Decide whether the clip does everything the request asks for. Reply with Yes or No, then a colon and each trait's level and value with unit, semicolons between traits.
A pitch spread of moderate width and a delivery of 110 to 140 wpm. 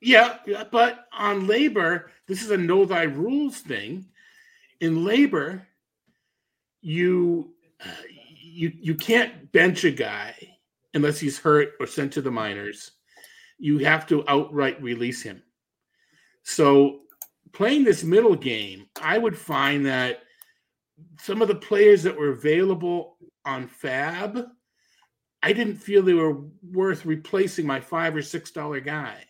No: wide, 5.8 semitones; slow, 135 wpm